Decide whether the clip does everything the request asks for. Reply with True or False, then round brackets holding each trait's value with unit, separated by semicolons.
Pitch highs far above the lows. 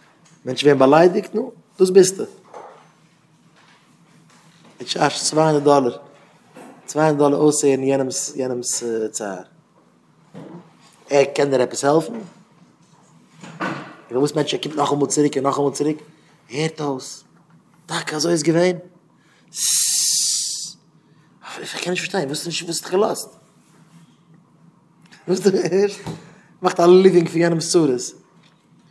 False (3.5 semitones)